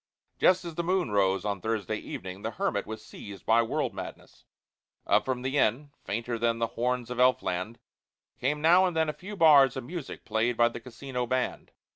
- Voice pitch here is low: Yes, low, 125 Hz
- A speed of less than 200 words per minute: No, fast, 205 wpm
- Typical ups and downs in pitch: Yes, average, 4.8 semitones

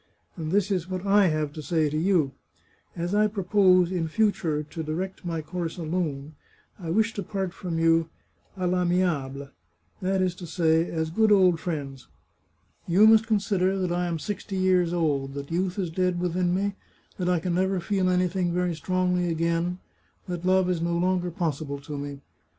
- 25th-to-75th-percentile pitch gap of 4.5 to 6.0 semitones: No, narrow, 2.5 semitones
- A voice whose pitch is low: No, medium, 175 Hz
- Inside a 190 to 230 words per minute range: Yes, average, 195 wpm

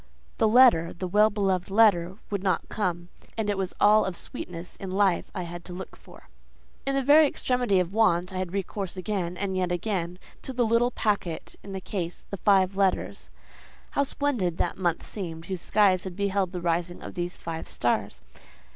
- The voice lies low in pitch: No, high, 190 Hz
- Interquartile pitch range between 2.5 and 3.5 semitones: Yes, average, 3.0 semitones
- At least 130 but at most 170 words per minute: No, average, 180 wpm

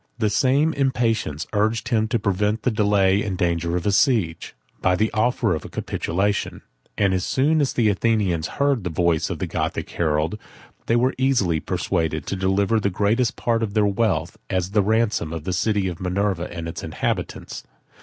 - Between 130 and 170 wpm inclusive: No, average, 185 wpm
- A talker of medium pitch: No, low, 100 Hz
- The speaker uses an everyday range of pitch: Yes, average, 4.2 semitones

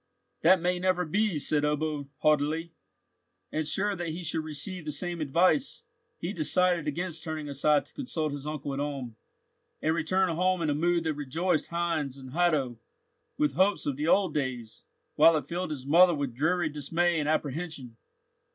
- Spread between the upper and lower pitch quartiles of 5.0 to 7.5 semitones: No, average, 3.2 semitones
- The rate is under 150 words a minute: No, average, 175 wpm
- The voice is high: No, medium, 155 Hz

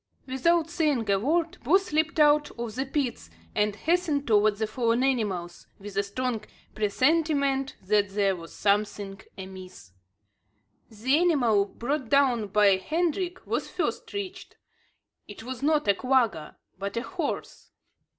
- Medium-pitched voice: No, high, 245 Hz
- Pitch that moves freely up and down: Yes, wide, 6.7 semitones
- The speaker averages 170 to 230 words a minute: No, average, 140 wpm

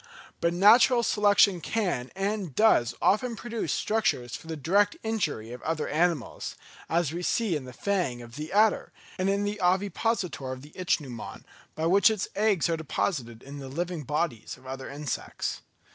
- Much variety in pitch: Yes, wide, 6.7 semitones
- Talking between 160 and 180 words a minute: Yes, average, 170 wpm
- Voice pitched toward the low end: No, medium, 170 Hz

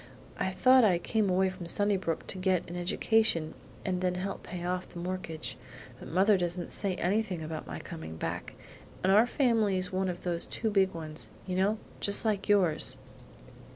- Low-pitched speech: No, medium, 185 Hz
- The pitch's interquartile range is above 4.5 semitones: No, narrow, 2.5 semitones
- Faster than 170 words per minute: Yes, average, 180 wpm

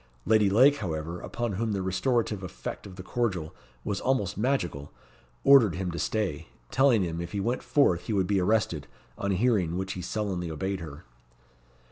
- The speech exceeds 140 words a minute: Yes, average, 175 wpm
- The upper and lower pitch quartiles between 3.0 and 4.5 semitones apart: Yes, average, 4.2 semitones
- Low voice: Yes, very low, 95 Hz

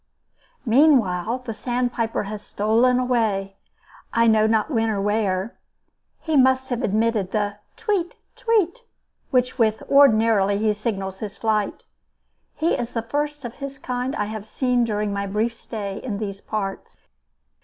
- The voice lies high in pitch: Yes, high, 225 Hz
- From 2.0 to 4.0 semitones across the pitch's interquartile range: Yes, average, 3.4 semitones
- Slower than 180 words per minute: Yes, average, 150 wpm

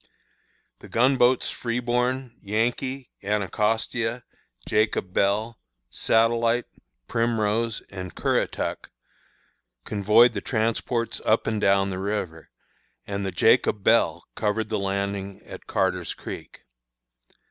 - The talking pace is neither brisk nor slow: No, slow, 105 wpm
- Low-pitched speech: Yes, low, 110 Hz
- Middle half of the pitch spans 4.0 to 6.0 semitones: No, average, 2.9 semitones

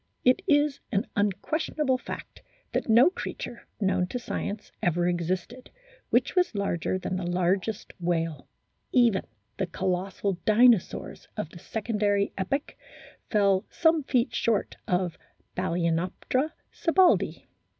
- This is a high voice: Yes, high, 205 Hz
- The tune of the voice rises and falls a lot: Yes, wide, 5.9 semitones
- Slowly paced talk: Yes, slow, 120 wpm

